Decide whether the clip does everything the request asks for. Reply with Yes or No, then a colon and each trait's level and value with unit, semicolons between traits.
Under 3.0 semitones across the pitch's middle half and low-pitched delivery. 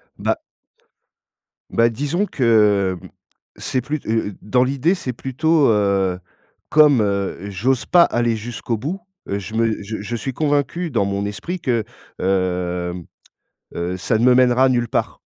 No: average, 5.0 semitones; low, 115 Hz